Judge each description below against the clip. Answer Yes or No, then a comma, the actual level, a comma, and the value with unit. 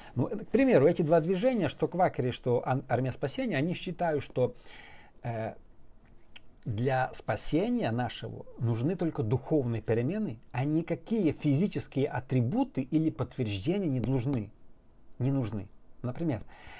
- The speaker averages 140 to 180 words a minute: No, average, 120 wpm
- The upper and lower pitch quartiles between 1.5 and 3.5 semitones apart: No, average, 4.9 semitones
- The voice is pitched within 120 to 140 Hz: Yes, low, 135 Hz